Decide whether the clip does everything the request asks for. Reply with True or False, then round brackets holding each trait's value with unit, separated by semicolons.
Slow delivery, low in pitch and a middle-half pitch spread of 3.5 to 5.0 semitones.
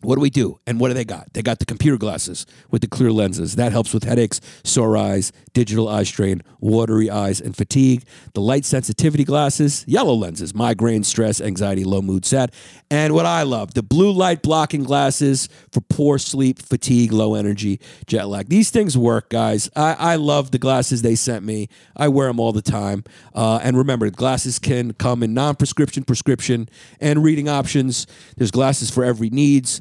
False (190 wpm; 125 Hz; 4.1 semitones)